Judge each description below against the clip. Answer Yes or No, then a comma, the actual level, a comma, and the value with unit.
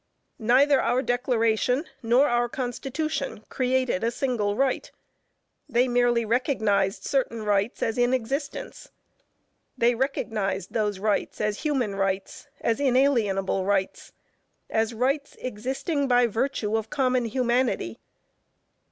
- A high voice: Yes, high, 240 Hz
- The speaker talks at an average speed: No, slow, 115 wpm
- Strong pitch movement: No, average, 3.4 semitones